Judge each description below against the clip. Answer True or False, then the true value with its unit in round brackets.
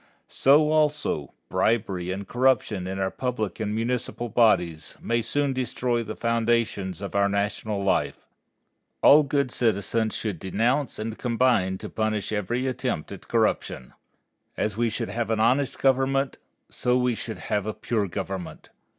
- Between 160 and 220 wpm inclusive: False (150 wpm)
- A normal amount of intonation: True (3.8 semitones)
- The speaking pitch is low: True (115 Hz)